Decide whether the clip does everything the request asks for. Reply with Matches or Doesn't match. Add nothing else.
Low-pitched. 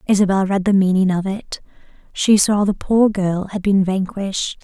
Doesn't match